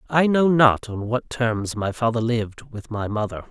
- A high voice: No, low, 120 Hz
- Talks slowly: No, fast, 205 wpm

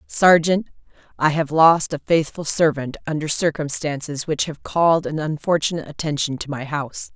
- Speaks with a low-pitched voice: No, medium, 155 Hz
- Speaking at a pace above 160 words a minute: No, average, 150 wpm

